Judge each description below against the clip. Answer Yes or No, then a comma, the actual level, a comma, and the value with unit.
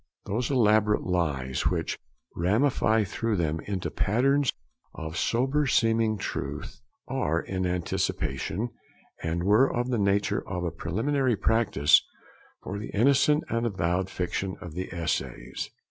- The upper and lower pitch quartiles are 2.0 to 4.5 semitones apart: No, average, 5.2 semitones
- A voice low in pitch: Yes, low, 100 Hz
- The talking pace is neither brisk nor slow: No, slow, 130 wpm